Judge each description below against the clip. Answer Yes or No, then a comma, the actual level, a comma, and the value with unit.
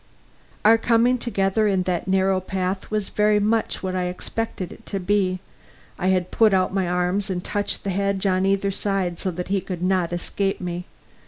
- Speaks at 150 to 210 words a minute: Yes, average, 190 wpm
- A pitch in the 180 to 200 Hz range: Yes, high, 190 Hz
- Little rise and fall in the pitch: Yes, narrow, 1.8 semitones